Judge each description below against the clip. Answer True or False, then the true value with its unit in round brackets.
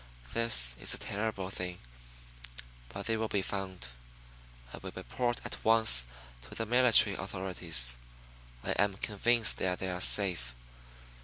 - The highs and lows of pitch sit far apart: False (3.8 semitones)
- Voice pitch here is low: True (95 Hz)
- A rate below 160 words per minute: True (140 wpm)